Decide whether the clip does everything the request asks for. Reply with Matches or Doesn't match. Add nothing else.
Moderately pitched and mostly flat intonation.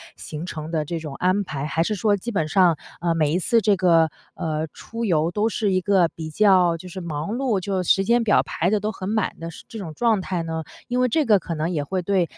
Doesn't match